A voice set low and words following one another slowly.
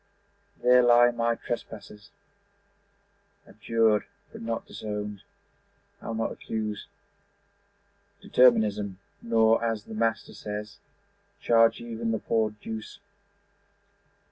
Yes: low, 110 Hz; slow, 90 wpm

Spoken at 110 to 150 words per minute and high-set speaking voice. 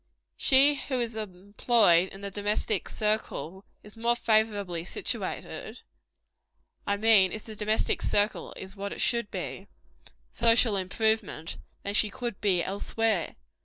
Yes: slow, 135 wpm; high, 210 Hz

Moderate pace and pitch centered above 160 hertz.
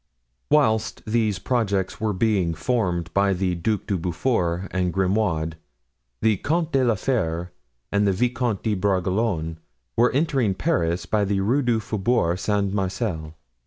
No: average, 145 wpm; low, 100 Hz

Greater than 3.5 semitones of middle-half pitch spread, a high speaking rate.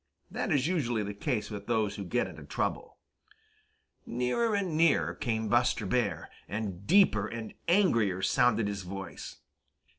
No: average, 4.6 semitones; average, 145 wpm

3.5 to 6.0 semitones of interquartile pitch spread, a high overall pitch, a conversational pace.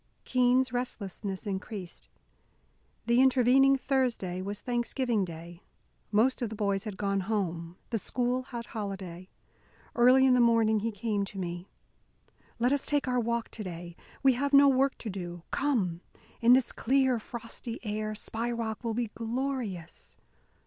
Yes: average, 4.3 semitones; high, 230 Hz; average, 150 wpm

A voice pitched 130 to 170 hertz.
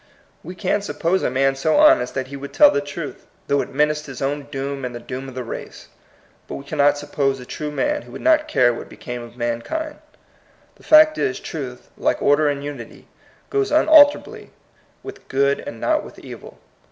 Yes: medium, 140 Hz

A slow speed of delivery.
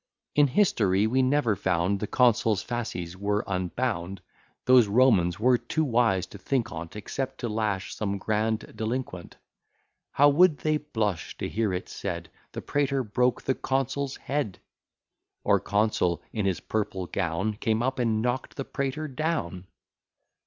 No: average, 150 wpm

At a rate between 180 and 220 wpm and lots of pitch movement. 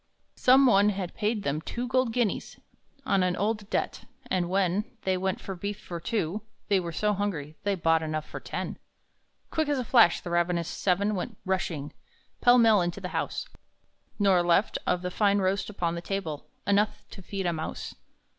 No: average, 185 wpm; average, 3.2 semitones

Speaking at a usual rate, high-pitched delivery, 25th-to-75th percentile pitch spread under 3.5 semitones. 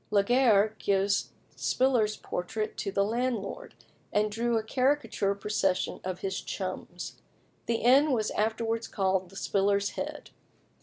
No: slow, 125 wpm; high, 210 Hz; average, 2.9 semitones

